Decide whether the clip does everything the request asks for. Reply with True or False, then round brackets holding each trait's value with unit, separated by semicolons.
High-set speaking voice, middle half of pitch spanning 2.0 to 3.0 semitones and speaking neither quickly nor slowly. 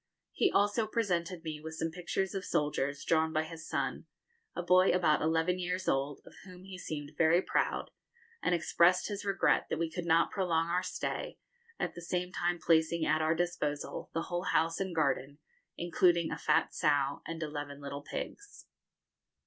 False (165 Hz; 2.5 semitones; 175 wpm)